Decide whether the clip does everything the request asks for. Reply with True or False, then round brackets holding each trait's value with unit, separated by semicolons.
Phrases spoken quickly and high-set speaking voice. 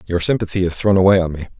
False (265 wpm; 90 Hz)